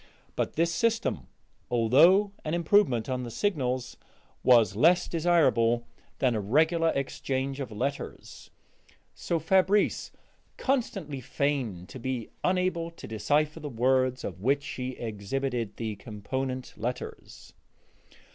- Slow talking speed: Yes, slow, 120 wpm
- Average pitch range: No, wide, 5.8 semitones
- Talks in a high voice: No, low, 135 Hz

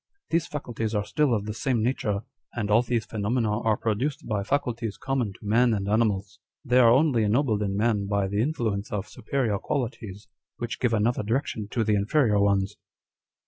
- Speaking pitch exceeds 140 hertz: No, low, 110 Hz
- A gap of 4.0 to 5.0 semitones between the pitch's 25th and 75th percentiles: No, average, 3.0 semitones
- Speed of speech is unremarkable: Yes, average, 185 wpm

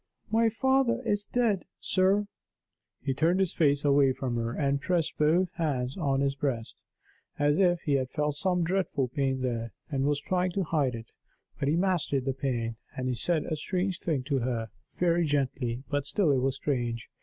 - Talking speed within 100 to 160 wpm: No, average, 190 wpm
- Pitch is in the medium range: Yes, medium, 145 Hz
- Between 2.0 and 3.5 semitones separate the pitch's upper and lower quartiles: No, average, 5.3 semitones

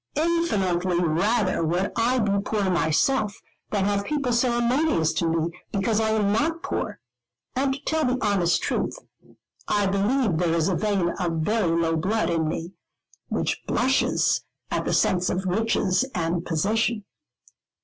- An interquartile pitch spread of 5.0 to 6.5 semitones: Yes, wide, 5.4 semitones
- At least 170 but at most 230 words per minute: No, average, 150 wpm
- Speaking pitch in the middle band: No, high, 200 Hz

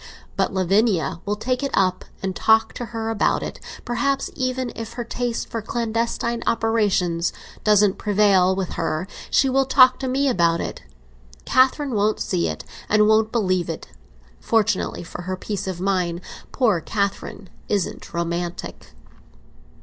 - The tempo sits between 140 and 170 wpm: Yes, average, 150 wpm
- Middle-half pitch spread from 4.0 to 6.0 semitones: Yes, average, 4.3 semitones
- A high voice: Yes, high, 210 Hz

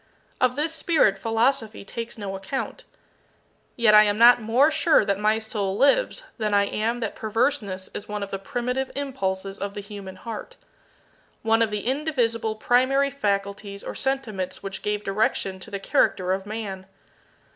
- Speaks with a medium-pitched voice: No, high, 215 Hz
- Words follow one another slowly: No, average, 165 wpm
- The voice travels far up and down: No, average, 3.9 semitones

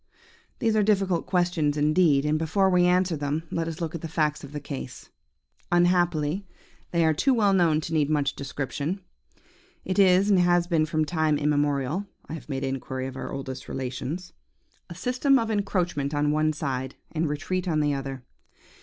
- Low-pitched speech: No, medium, 155 Hz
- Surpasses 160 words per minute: Yes, average, 180 wpm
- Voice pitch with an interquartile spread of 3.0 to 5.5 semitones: Yes, average, 3.7 semitones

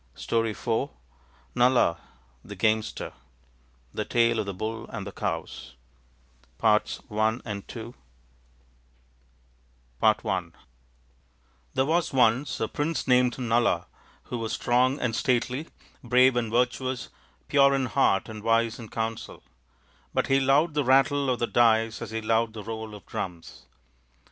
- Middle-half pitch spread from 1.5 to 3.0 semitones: Yes, narrow, 2.6 semitones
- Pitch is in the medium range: No, low, 115 Hz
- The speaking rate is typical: No, slow, 130 wpm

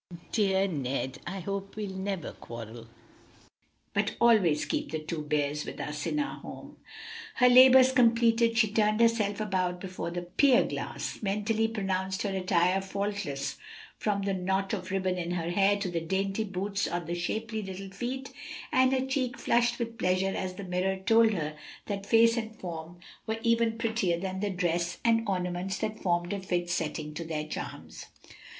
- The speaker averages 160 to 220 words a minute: Yes, average, 170 wpm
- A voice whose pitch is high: Yes, high, 195 Hz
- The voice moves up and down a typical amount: Yes, average, 4.1 semitones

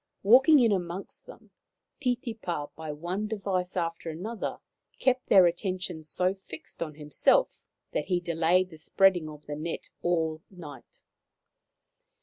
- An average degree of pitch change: Yes, average, 3.5 semitones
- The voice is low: No, medium, 175 Hz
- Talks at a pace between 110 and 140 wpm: Yes, slow, 135 wpm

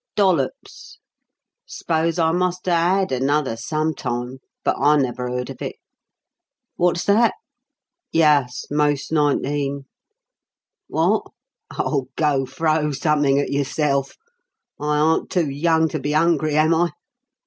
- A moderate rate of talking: No, slow, 120 wpm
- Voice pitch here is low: No, medium, 150 Hz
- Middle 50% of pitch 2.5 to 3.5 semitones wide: Yes, average, 2.9 semitones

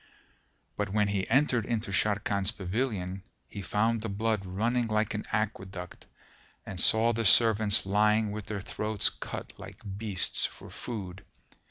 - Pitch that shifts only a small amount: Yes, narrow, 2.2 semitones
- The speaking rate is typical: Yes, average, 145 wpm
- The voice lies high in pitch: No, low, 105 Hz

